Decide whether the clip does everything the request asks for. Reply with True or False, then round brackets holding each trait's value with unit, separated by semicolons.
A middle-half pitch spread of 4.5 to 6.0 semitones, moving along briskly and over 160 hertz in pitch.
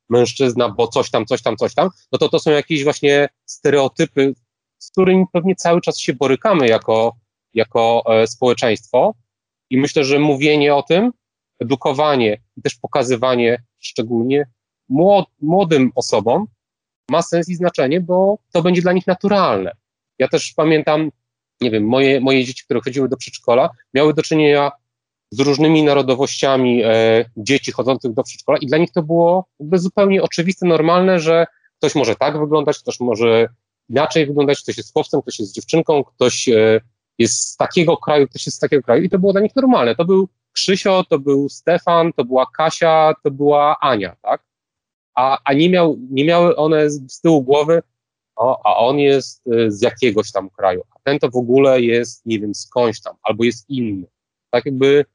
False (5.1 semitones; 175 wpm; 140 Hz)